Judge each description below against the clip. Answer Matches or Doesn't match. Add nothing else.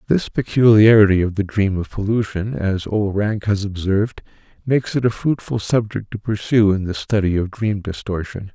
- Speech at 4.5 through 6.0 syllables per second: Matches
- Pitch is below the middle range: Matches